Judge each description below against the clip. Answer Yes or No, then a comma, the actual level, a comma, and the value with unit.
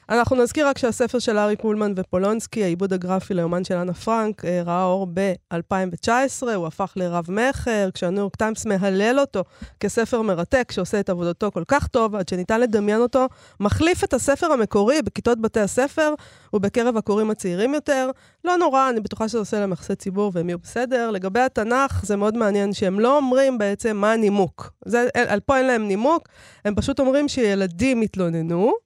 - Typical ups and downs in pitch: Yes, average, 4.4 semitones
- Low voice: No, high, 215 Hz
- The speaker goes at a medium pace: No, fast, 175 wpm